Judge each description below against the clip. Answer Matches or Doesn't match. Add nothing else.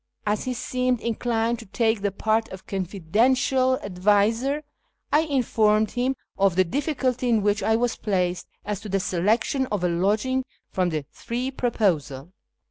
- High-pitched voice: Matches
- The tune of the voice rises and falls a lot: Doesn't match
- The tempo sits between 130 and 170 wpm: Matches